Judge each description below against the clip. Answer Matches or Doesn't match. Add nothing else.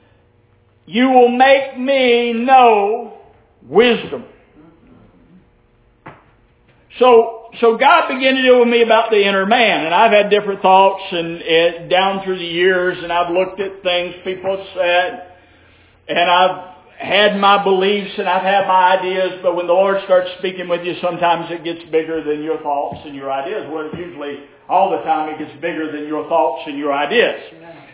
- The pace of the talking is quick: Doesn't match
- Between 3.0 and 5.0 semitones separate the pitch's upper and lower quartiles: Matches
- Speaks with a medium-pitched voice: Matches